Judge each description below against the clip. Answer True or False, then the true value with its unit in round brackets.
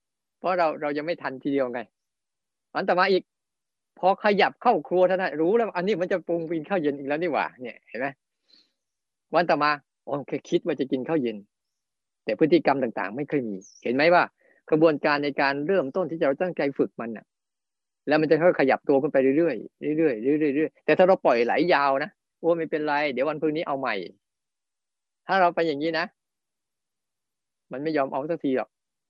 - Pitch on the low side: False (155 Hz)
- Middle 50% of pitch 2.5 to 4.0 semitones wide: True (3.7 semitones)